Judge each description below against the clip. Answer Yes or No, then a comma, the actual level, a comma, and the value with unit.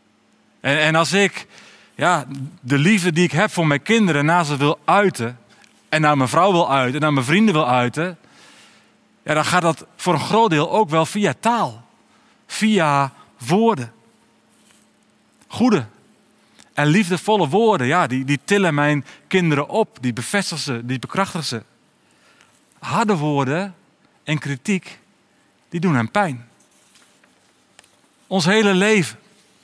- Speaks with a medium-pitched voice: Yes, medium, 170 Hz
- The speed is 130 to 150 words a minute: Yes, average, 140 wpm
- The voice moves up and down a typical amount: No, wide, 6.2 semitones